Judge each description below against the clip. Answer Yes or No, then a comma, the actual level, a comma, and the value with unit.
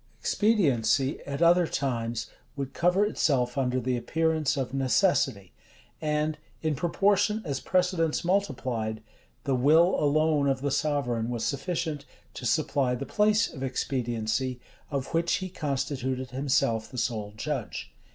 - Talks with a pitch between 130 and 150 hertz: Yes, medium, 140 Hz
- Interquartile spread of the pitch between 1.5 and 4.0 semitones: No, average, 4.5 semitones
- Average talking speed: No, slow, 130 wpm